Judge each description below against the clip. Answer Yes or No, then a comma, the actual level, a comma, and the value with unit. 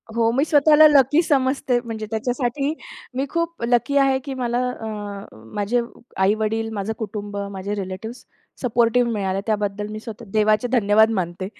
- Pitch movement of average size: Yes, average, 3.8 semitones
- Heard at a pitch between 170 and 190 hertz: No, high, 230 Hz